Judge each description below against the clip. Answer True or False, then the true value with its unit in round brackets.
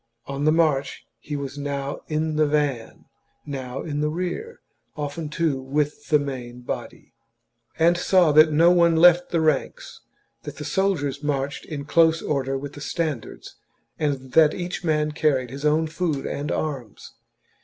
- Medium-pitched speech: True (150 Hz)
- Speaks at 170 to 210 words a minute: False (160 wpm)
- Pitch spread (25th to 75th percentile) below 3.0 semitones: True (2.6 semitones)